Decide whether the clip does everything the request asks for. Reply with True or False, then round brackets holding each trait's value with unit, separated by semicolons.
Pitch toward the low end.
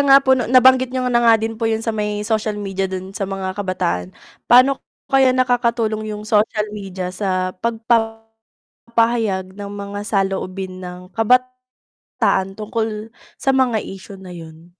False (215 Hz)